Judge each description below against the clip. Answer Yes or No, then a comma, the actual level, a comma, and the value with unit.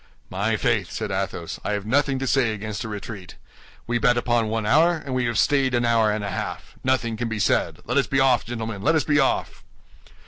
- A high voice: No, low, 115 Hz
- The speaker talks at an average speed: No, fast, 230 wpm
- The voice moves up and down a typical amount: Yes, average, 3.8 semitones